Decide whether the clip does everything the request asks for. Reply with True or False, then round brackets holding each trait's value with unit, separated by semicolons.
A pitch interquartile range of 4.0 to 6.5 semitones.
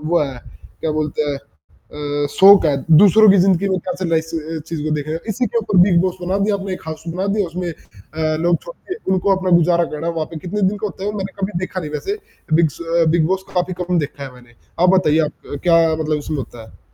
False (3.5 semitones)